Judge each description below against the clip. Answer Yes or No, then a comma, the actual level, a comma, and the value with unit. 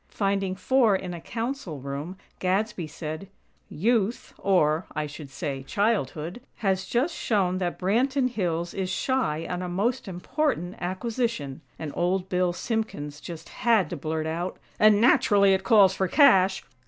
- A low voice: No, high, 190 Hz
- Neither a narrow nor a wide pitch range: Yes, average, 4.9 semitones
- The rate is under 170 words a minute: Yes, average, 150 wpm